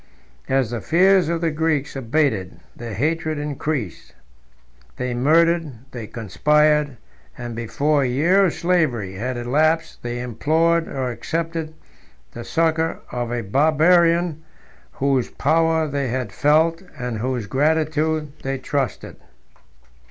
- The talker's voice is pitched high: No, medium, 150 Hz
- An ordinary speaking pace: No, slow, 120 wpm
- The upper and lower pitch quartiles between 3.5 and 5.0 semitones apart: Yes, average, 4.6 semitones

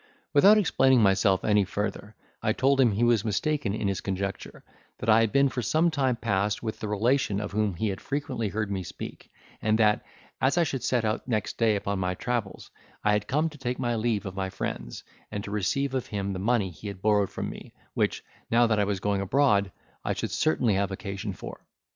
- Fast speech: Yes, fast, 220 wpm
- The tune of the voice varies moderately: Yes, average, 3.6 semitones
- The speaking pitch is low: Yes, low, 105 Hz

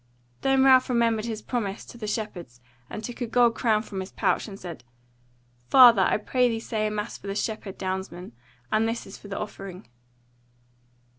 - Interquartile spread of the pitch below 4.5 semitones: Yes, average, 3.2 semitones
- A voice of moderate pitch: No, high, 215 Hz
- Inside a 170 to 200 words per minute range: Yes, average, 190 wpm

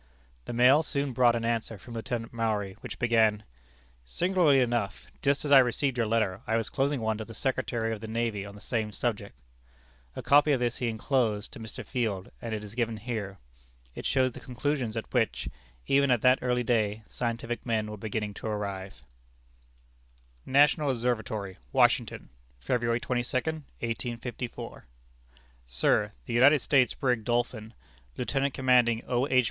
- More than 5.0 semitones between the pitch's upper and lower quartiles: No, average, 2.8 semitones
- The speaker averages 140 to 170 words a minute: Yes, average, 165 wpm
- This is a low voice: Yes, low, 120 Hz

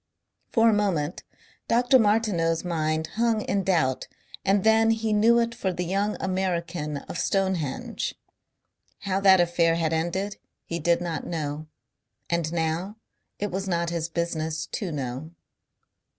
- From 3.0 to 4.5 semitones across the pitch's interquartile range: Yes, average, 4.0 semitones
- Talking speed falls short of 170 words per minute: Yes, average, 140 wpm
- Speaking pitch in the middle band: Yes, medium, 175 Hz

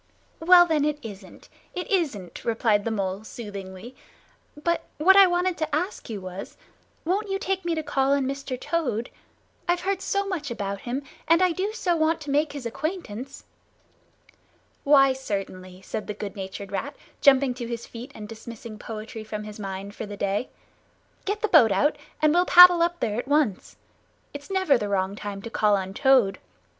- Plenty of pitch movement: Yes, wide, 8.1 semitones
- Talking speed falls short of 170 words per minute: No, average, 185 wpm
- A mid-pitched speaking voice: No, very high, 260 Hz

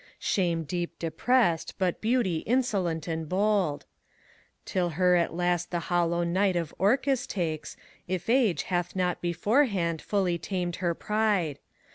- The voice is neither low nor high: Yes, medium, 180 Hz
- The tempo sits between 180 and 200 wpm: No, slow, 135 wpm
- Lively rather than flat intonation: No, average, 3.2 semitones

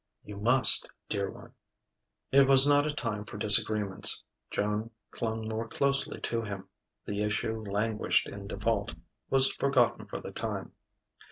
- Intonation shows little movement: No, average, 3.2 semitones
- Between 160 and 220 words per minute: No, average, 145 wpm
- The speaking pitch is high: No, low, 110 Hz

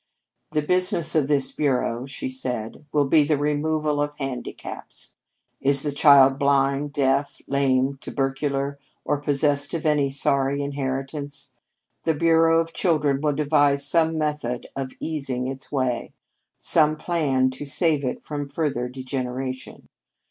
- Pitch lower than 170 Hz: Yes, medium, 140 Hz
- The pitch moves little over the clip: Yes, narrow, 1.9 semitones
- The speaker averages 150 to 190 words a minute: No, slow, 135 wpm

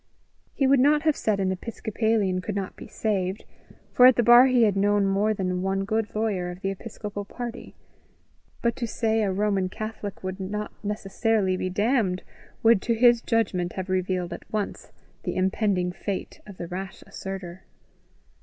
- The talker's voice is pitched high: Yes, high, 205 Hz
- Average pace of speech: Yes, average, 175 wpm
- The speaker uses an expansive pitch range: No, average, 3.0 semitones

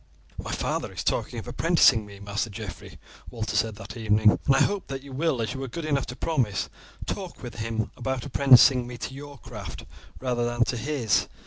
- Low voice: Yes, low, 120 Hz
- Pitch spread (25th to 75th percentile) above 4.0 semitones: No, average, 3.6 semitones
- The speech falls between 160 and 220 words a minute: Yes, average, 200 wpm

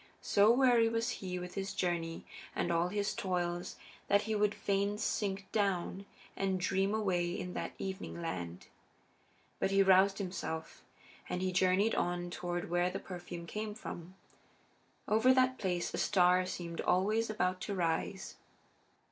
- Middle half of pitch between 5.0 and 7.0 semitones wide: No, average, 2.7 semitones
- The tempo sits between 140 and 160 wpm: Yes, average, 150 wpm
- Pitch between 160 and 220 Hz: Yes, high, 190 Hz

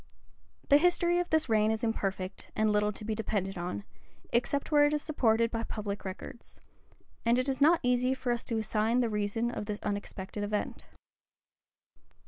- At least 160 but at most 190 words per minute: Yes, average, 175 wpm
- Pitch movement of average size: Yes, average, 3.6 semitones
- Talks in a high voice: Yes, high, 225 Hz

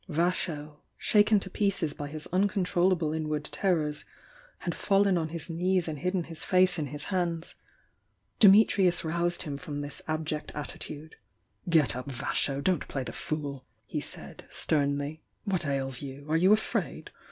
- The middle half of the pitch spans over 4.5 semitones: No, average, 3.8 semitones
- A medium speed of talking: Yes, average, 155 wpm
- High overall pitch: No, medium, 160 Hz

